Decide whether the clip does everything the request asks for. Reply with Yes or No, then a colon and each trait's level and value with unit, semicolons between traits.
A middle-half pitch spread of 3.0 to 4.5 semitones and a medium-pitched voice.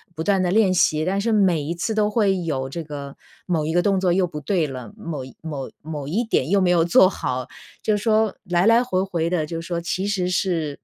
Yes: average, 4.0 semitones; medium, 175 Hz